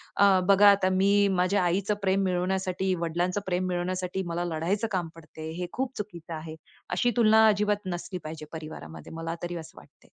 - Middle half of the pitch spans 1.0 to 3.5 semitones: Yes, average, 2.8 semitones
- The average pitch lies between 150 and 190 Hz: Yes, medium, 185 Hz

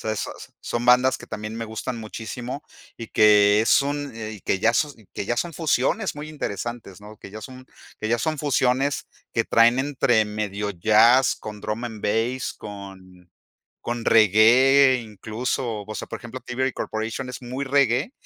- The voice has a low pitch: Yes, low, 115 Hz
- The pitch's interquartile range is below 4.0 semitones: Yes, average, 3.3 semitones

